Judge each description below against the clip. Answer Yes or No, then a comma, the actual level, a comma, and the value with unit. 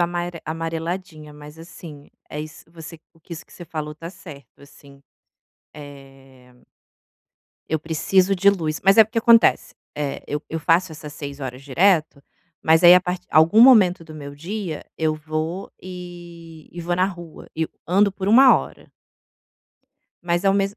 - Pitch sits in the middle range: Yes, medium, 165 Hz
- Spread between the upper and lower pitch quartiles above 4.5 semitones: No, average, 3.2 semitones